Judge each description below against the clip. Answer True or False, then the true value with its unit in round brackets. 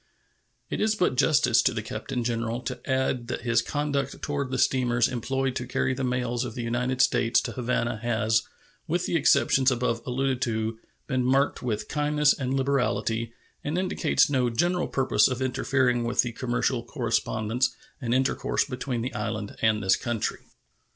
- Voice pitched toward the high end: False (125 Hz)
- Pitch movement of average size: False (2.3 semitones)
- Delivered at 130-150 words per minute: False (170 wpm)